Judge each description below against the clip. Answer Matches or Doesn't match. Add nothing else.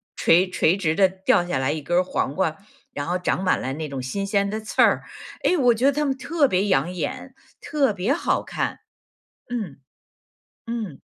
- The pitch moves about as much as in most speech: Doesn't match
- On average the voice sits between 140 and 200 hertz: Matches